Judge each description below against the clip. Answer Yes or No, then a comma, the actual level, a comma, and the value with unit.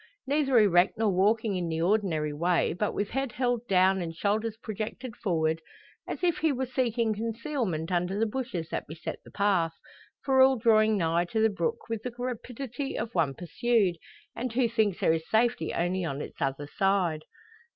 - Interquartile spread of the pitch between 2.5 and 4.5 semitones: No, wide, 5.6 semitones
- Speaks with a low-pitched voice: No, high, 210 Hz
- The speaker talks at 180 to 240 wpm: Yes, average, 185 wpm